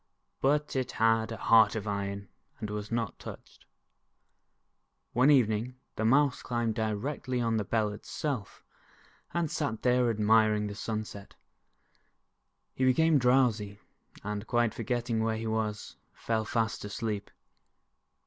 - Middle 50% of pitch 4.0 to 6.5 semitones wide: No, average, 2.7 semitones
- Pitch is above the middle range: No, low, 110 Hz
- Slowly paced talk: Yes, slow, 130 wpm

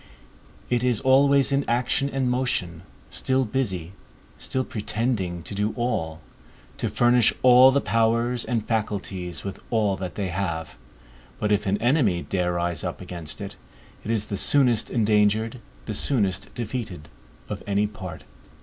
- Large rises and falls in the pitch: No, average, 4.7 semitones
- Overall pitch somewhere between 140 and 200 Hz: No, low, 110 Hz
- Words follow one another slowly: No, average, 150 wpm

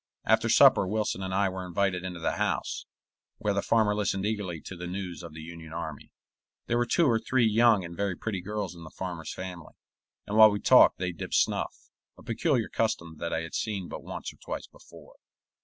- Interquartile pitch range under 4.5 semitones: Yes, average, 4.0 semitones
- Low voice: Yes, very low, 95 Hz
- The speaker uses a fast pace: Yes, fast, 210 wpm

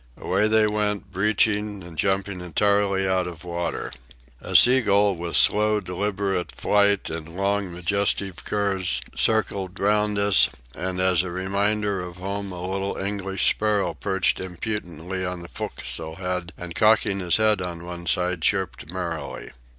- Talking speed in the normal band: Yes, average, 150 wpm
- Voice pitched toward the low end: Yes, very low, 95 Hz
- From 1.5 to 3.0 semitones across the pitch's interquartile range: Yes, narrow, 2.4 semitones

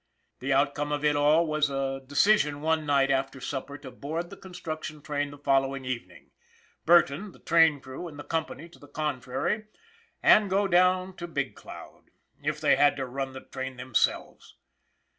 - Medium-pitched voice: Yes, medium, 145 Hz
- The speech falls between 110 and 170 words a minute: No, average, 180 wpm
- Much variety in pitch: No, average, 3.3 semitones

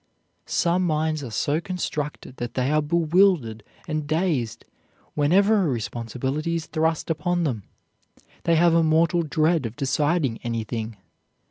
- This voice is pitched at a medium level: Yes, medium, 155 Hz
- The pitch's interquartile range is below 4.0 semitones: No, average, 4.5 semitones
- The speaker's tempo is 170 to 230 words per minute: No, slow, 135 wpm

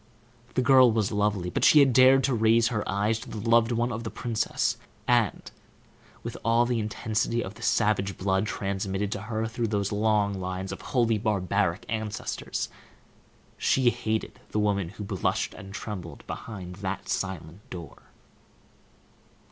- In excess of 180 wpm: No, average, 155 wpm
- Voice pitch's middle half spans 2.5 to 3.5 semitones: Yes, average, 2.9 semitones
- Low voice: Yes, low, 105 Hz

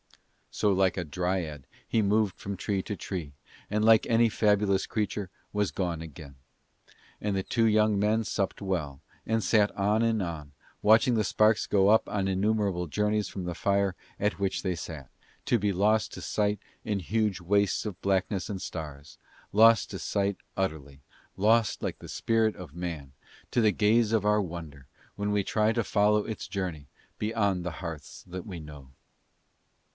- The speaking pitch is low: Yes, low, 100 Hz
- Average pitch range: Yes, average, 3.3 semitones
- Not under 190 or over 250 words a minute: No, average, 170 wpm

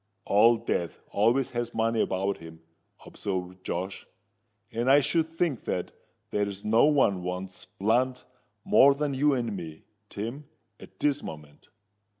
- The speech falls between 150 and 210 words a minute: No, average, 140 wpm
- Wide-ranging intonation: Yes, wide, 6.3 semitones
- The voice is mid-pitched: No, low, 110 Hz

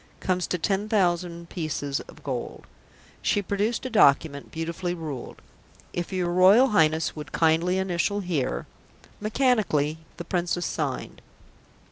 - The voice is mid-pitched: Yes, medium, 175 Hz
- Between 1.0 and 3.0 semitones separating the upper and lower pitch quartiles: No, average, 3.5 semitones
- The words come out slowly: Yes, slow, 130 wpm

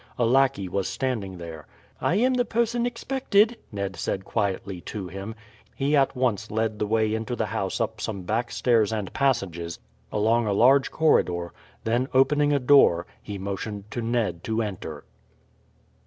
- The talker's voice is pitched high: No, low, 110 Hz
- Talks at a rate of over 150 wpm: Yes, average, 165 wpm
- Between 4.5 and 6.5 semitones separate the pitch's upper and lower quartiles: Yes, average, 5.2 semitones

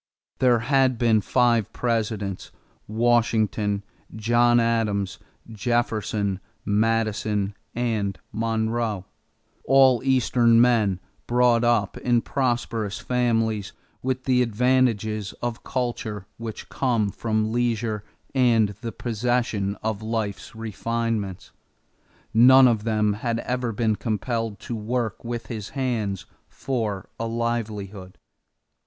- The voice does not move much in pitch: Yes, narrow, 2.2 semitones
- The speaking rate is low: Yes, slow, 105 wpm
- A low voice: Yes, low, 115 Hz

